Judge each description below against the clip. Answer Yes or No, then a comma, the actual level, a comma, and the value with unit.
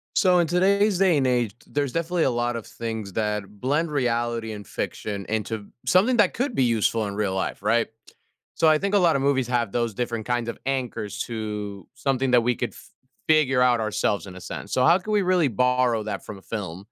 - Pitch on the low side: Yes, low, 120 Hz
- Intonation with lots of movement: Yes, wide, 6.1 semitones